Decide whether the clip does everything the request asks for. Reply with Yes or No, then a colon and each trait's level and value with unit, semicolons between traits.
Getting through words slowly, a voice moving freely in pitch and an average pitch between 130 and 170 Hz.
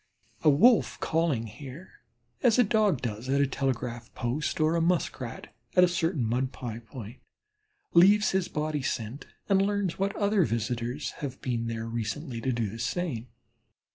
No: average, 165 wpm; wide, 7.1 semitones; low, 135 Hz